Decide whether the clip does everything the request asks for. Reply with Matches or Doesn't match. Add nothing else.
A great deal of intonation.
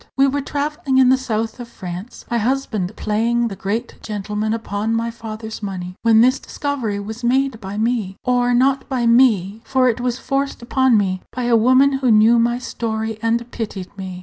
Doesn't match